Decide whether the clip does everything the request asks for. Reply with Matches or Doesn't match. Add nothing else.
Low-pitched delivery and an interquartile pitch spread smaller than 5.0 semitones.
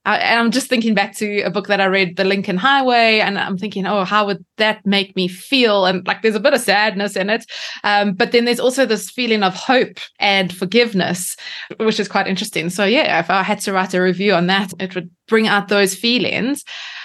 Doesn't match